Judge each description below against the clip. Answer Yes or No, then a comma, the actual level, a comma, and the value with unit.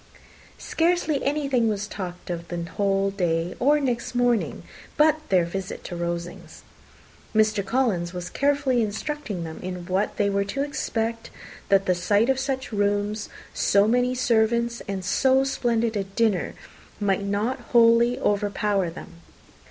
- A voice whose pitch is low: No, high, 210 Hz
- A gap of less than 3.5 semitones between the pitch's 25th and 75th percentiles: No, average, 4.4 semitones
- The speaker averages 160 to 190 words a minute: No, average, 145 wpm